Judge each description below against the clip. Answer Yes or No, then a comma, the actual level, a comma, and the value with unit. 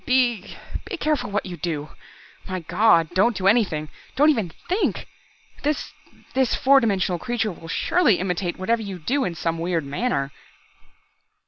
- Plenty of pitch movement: Yes, wide, 6.5 semitones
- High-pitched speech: Yes, high, 195 Hz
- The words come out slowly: No, average, 150 wpm